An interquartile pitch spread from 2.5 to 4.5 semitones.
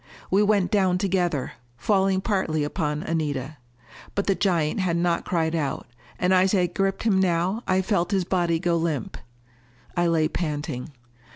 Yes: average, 3.0 semitones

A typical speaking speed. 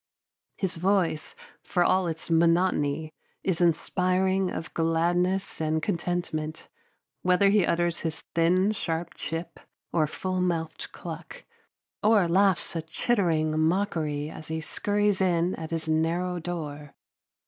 No: slow, 125 wpm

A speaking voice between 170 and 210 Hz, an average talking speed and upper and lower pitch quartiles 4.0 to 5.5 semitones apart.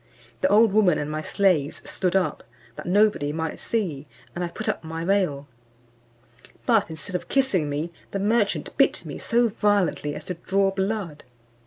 Yes: medium, 185 Hz; average, 170 wpm; average, 4.5 semitones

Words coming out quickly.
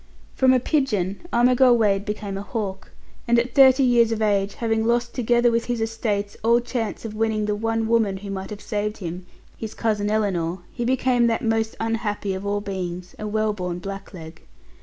No: average, 190 wpm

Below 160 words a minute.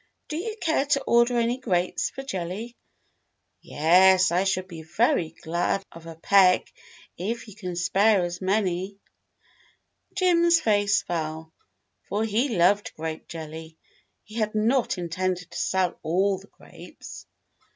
Yes: average, 140 wpm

